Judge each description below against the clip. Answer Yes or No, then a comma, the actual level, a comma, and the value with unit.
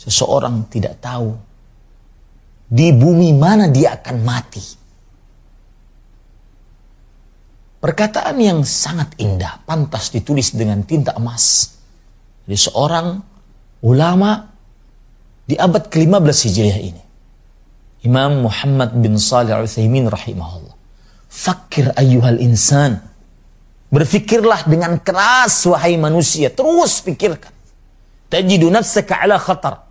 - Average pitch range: No, wide, 7.7 semitones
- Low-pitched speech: Yes, low, 130 Hz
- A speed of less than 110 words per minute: Yes, average, 90 wpm